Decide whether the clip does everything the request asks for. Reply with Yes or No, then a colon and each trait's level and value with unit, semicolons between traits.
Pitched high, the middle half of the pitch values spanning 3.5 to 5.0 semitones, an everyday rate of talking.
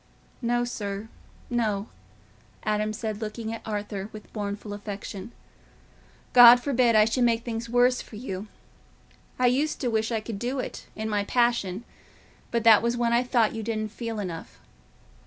No: high, 225 Hz; narrow, 2.4 semitones; average, 155 wpm